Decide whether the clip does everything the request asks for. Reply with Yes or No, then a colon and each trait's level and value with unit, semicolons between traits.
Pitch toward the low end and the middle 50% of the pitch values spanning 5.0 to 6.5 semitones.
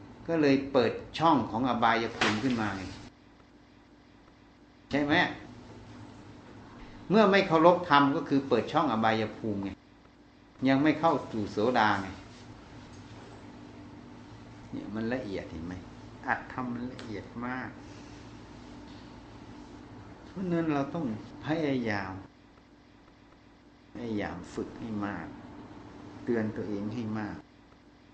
Yes: low, 115 Hz; wide, 5.6 semitones